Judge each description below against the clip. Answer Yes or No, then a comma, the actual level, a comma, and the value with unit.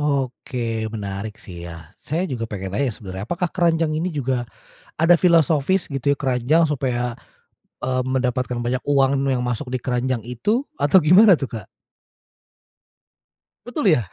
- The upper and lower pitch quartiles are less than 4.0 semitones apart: No, average, 4.6 semitones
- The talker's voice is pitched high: No, low, 130 Hz